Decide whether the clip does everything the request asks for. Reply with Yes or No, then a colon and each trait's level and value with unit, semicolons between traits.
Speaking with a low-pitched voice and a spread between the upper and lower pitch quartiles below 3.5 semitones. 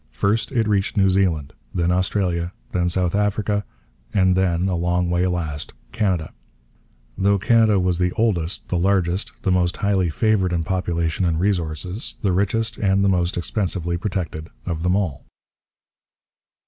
Yes: very low, 90 Hz; narrow, 2.5 semitones